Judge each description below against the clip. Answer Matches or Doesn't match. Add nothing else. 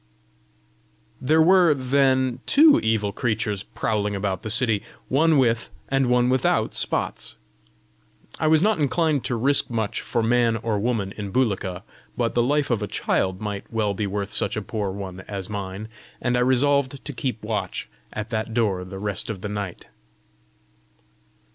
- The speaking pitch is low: Matches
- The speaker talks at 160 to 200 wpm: Matches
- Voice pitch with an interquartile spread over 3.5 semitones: Matches